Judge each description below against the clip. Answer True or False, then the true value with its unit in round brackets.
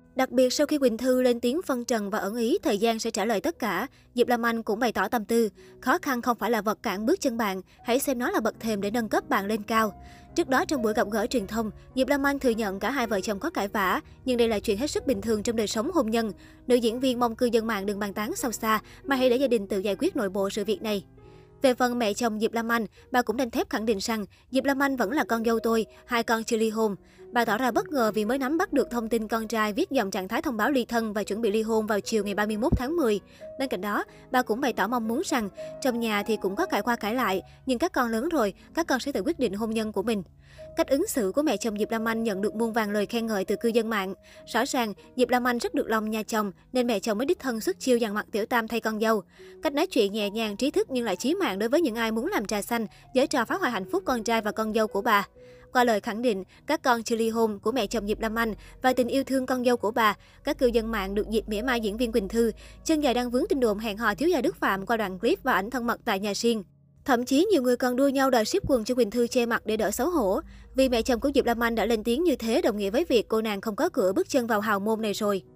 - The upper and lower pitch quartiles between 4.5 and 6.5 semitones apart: False (3.2 semitones)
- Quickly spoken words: True (305 wpm)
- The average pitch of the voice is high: True (235 Hz)